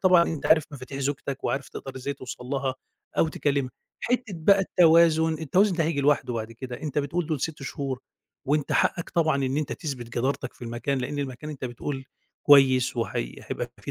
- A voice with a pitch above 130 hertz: Yes, medium, 140 Hz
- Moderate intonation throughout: Yes, average, 3.5 semitones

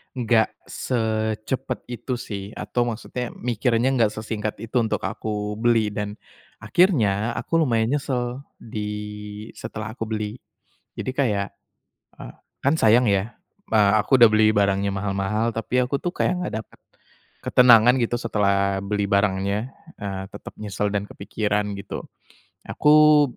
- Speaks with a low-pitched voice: Yes, low, 110 Hz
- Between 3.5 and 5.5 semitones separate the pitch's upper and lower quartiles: No, average, 2.9 semitones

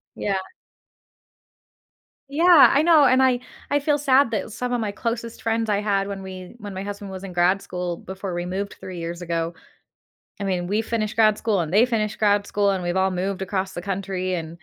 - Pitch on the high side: Yes, high, 200 Hz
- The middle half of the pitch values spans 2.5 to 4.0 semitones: Yes, average, 3.5 semitones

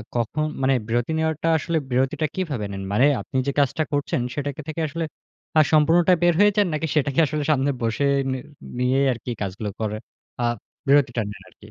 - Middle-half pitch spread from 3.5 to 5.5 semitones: Yes, average, 4.4 semitones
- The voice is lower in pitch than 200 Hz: Yes, medium, 140 Hz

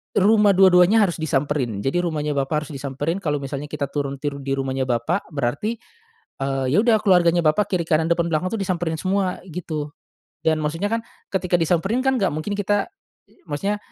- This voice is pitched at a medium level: Yes, medium, 165 Hz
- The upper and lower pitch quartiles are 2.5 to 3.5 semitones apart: No, average, 5.1 semitones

